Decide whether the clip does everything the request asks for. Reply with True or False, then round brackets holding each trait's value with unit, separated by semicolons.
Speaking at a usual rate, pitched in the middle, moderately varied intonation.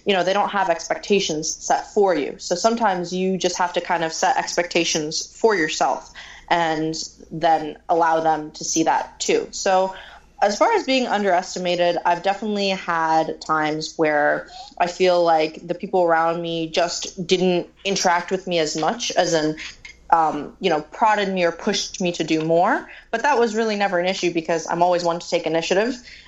True (185 wpm; 175 Hz; 3.1 semitones)